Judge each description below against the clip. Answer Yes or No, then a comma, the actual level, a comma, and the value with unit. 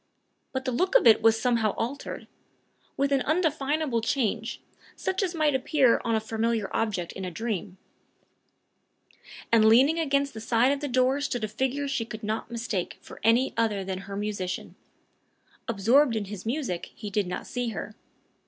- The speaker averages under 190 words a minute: Yes, average, 170 wpm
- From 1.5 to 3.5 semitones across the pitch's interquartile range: No, average, 4.3 semitones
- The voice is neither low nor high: No, high, 230 Hz